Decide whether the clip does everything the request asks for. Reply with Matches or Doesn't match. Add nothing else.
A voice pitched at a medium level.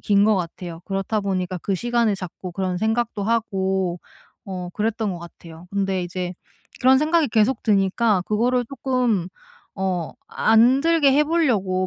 Doesn't match